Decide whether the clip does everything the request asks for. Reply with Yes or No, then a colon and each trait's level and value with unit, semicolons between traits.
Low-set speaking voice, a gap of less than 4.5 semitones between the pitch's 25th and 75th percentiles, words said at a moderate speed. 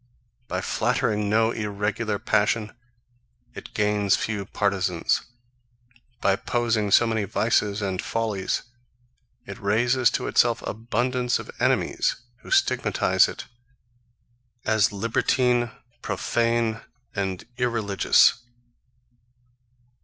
No: low, 110 Hz; narrow, 2.6 semitones; slow, 95 wpm